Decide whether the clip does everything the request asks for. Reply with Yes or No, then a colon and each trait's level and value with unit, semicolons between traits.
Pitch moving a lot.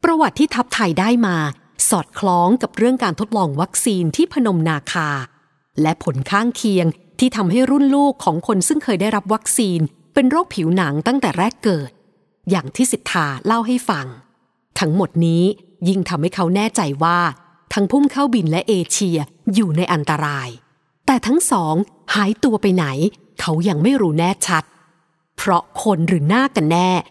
Yes: wide, 5.7 semitones